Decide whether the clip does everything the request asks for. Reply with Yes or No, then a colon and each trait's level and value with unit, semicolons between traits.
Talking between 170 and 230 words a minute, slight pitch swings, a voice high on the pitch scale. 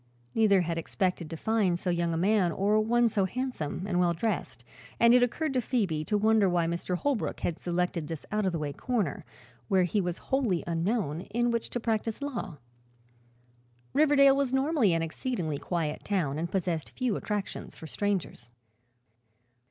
No: average, 175 wpm; wide, 5.5 semitones; high, 195 Hz